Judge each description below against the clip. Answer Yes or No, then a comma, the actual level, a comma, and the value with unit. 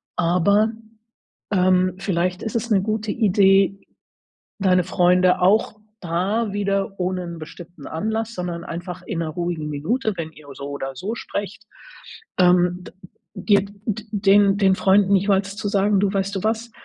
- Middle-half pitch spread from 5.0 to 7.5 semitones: No, narrow, 2.6 semitones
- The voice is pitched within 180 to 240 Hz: Yes, high, 190 Hz